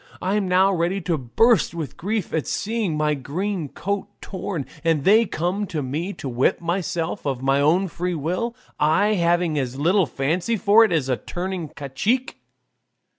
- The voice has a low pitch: No, medium, 175 Hz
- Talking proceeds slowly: No, average, 175 wpm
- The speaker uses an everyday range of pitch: Yes, average, 4.7 semitones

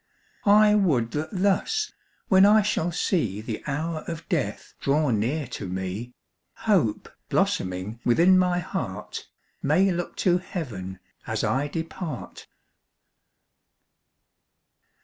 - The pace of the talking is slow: Yes, slow, 110 wpm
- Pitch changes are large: Yes, wide, 8.5 semitones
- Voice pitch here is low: No, medium, 160 Hz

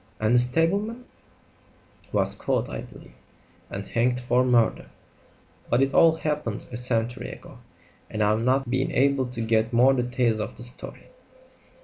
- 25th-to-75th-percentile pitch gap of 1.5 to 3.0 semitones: Yes, narrow, 2.6 semitones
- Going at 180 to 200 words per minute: No, average, 155 wpm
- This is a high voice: No, low, 125 Hz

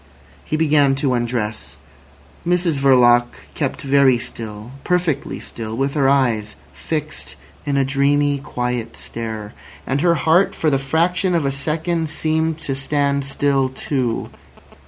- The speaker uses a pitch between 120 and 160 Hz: Yes, medium, 140 Hz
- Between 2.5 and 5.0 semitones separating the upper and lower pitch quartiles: Yes, average, 3.8 semitones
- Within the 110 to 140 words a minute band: Yes, slow, 135 wpm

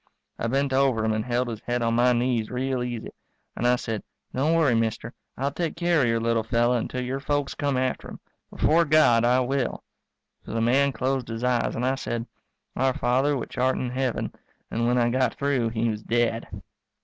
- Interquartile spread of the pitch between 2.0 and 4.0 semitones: Yes, narrow, 2.4 semitones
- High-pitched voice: No, low, 125 Hz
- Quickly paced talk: Yes, fast, 210 wpm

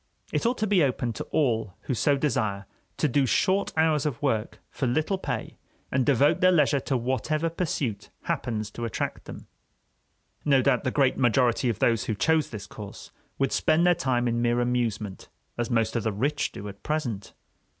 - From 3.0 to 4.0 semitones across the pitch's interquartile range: No, average, 4.7 semitones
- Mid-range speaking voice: No, low, 130 Hz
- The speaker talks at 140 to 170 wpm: No, average, 190 wpm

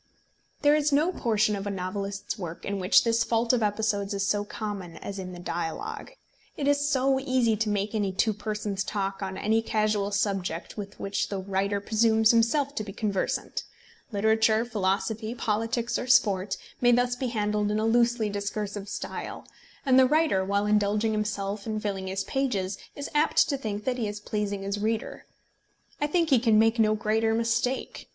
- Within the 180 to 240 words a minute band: Yes, average, 185 wpm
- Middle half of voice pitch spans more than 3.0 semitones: No, average, 2.7 semitones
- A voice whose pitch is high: Yes, high, 215 Hz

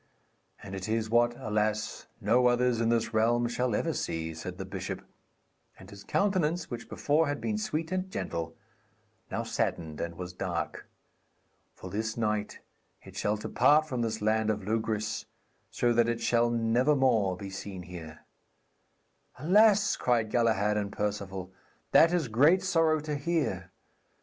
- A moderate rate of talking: Yes, average, 155 wpm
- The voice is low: Yes, low, 115 Hz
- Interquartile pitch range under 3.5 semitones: No, average, 5.1 semitones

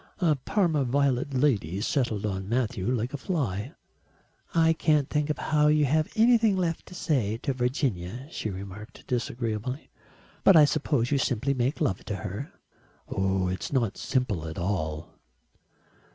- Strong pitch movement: Yes, wide, 6.5 semitones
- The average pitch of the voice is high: No, low, 125 Hz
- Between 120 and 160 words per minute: Yes, average, 150 wpm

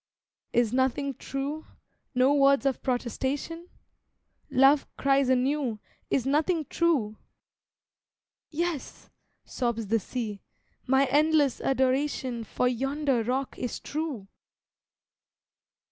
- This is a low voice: No, very high, 270 Hz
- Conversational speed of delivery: No, slow, 95 wpm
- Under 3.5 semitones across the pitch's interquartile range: Yes, average, 2.7 semitones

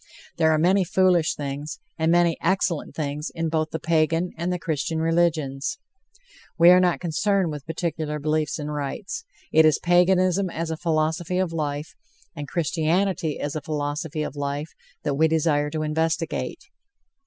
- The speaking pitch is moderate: Yes, medium, 160 Hz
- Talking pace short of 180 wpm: Yes, average, 160 wpm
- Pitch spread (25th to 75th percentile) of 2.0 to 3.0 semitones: Yes, narrow, 2.4 semitones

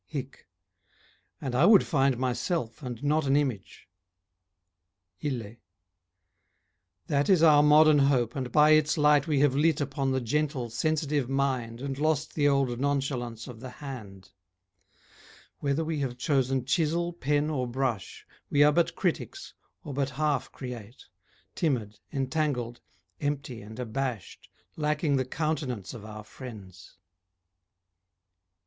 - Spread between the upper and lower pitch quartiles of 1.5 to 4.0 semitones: Yes, average, 3.5 semitones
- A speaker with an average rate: No, slow, 130 wpm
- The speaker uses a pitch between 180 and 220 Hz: No, low, 135 Hz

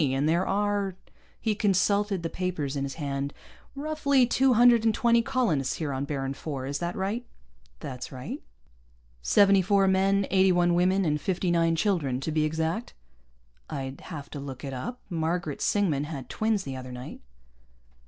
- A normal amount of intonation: No, wide, 6.2 semitones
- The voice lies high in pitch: No, medium, 175 Hz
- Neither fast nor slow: Yes, average, 175 wpm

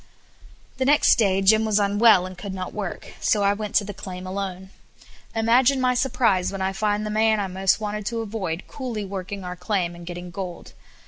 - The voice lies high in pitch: Yes, high, 200 Hz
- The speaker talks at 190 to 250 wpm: Yes, average, 200 wpm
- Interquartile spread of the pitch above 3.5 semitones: No, average, 2.7 semitones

